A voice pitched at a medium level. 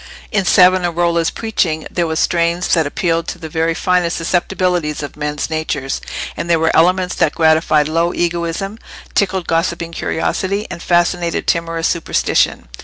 Yes: medium, 170 Hz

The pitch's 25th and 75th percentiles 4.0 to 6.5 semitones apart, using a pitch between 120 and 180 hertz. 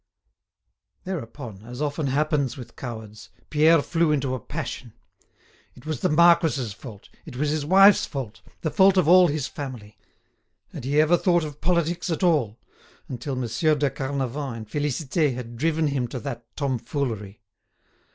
Yes: average, 4.4 semitones; medium, 140 Hz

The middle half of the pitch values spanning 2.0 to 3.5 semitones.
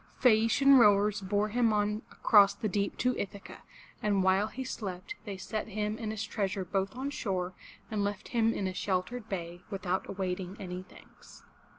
Yes: narrow, 2.4 semitones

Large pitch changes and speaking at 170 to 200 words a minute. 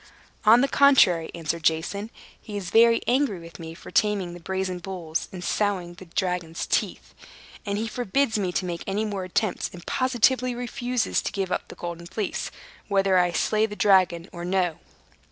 No: average, 4.0 semitones; average, 180 wpm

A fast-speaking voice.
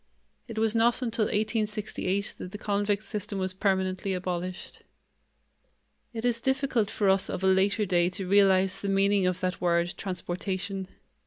No: average, 155 wpm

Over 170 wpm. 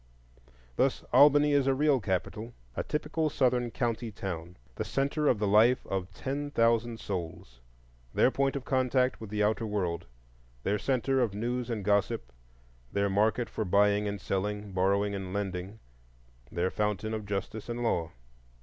No: average, 155 wpm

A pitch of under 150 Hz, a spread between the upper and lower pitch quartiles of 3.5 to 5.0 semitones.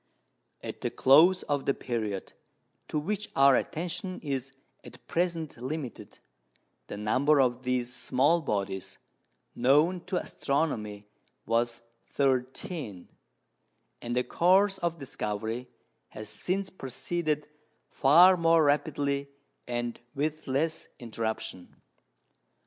No: medium, 140 Hz; wide, 5.4 semitones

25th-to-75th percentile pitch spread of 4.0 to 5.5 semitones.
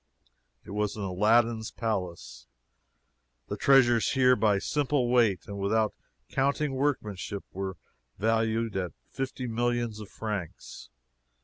No: average, 3.3 semitones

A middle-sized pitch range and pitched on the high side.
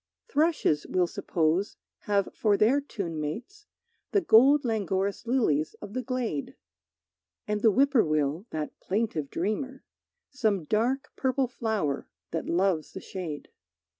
No: wide, 7.3 semitones; high, 210 Hz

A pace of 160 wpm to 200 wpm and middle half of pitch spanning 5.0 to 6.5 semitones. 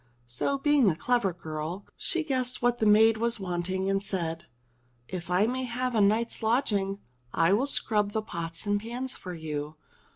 Yes: average, 175 wpm; average, 5.3 semitones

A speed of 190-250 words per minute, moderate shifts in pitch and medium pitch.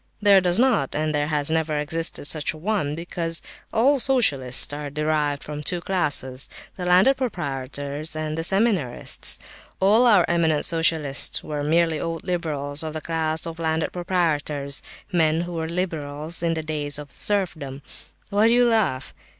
No: average, 160 wpm; average, 3.2 semitones; medium, 160 Hz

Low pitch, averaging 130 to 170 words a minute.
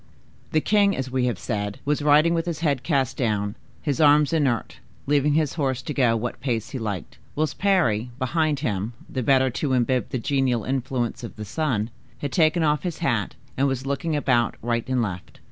No: low, 130 Hz; average, 195 wpm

